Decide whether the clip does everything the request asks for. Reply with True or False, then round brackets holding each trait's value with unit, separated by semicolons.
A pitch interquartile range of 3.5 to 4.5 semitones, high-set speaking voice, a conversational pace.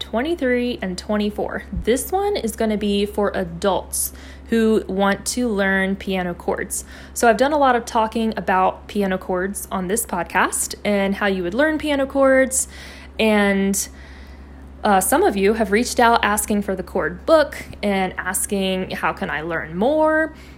True (3.8 semitones; 205 Hz; 165 wpm)